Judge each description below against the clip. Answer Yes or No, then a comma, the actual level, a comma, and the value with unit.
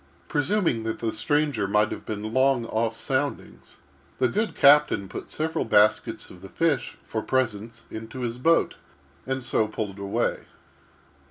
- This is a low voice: Yes, low, 115 Hz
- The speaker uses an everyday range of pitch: Yes, average, 4.4 semitones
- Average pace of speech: Yes, average, 150 wpm